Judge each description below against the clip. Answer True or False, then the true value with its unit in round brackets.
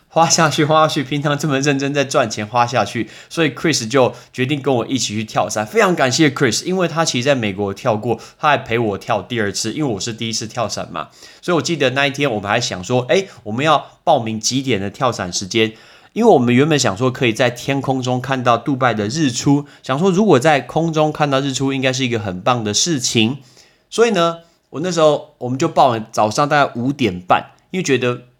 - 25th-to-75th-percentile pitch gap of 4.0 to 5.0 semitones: True (4.3 semitones)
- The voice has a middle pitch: False (130 Hz)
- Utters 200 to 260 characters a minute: False (345 characters per minute)